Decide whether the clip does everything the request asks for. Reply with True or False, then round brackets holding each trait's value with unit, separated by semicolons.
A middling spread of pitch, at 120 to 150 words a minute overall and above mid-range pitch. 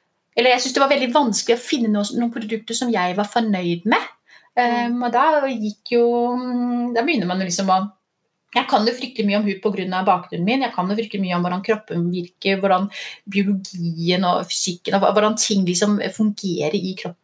False (4.4 semitones; 200 wpm; 210 Hz)